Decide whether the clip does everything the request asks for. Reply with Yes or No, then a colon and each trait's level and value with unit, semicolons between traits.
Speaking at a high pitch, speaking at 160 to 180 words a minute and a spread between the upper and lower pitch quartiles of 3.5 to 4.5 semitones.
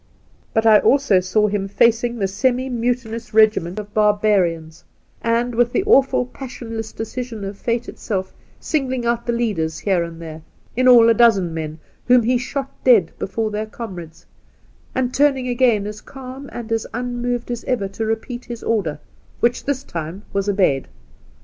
Yes: high, 225 Hz; average, 175 wpm; average, 3.8 semitones